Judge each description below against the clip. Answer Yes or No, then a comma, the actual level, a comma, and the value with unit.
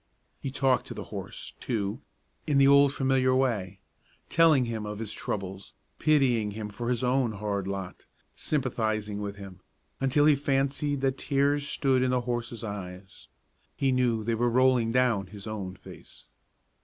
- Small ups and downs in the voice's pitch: No, average, 4.5 semitones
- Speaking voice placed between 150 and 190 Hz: No, low, 120 Hz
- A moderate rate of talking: Yes, average, 160 wpm